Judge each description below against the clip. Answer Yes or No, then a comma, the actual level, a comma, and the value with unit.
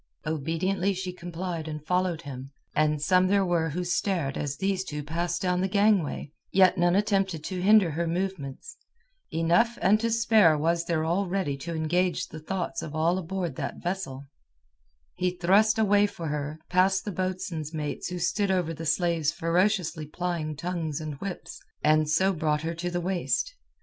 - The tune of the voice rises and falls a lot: No, average, 3.3 semitones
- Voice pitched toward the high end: No, medium, 175 Hz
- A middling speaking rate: Yes, average, 175 wpm